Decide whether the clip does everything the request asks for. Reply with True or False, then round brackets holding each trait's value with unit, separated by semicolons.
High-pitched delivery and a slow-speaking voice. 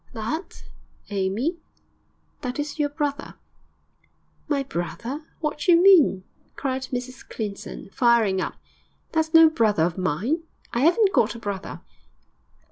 True (260 Hz; 125 wpm)